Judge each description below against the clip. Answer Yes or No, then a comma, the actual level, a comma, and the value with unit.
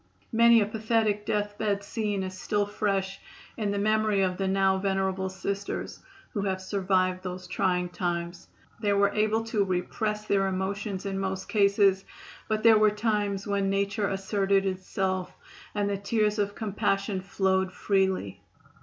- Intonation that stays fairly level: Yes, narrow, 1.6 semitones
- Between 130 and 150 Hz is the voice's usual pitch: No, high, 200 Hz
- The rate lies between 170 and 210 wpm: No, average, 155 wpm